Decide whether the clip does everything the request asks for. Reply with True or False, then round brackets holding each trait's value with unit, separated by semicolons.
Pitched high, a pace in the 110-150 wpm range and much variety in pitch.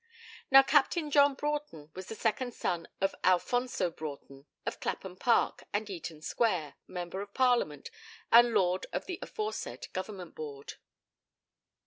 True (200 Hz; 135 wpm; 6.9 semitones)